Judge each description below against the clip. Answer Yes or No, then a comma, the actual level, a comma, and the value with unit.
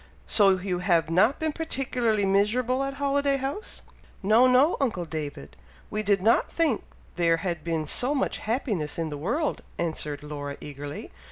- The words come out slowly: No, average, 160 wpm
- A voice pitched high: Yes, high, 200 Hz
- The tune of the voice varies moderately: No, wide, 8.2 semitones